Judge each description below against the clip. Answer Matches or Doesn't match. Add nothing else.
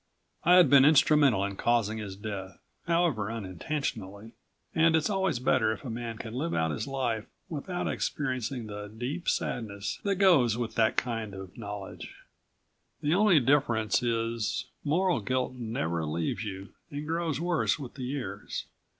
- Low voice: Matches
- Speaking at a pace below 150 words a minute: Doesn't match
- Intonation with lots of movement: Matches